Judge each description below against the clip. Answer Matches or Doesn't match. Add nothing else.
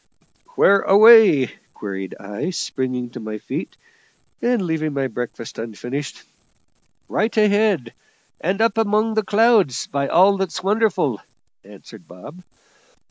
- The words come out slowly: Matches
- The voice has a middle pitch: Matches